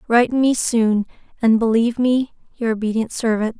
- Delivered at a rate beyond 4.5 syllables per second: Yes, 4.8 syllables/s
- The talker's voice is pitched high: Yes, high, 230 Hz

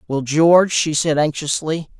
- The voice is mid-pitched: Yes, medium, 155 Hz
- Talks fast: No, average, 150 wpm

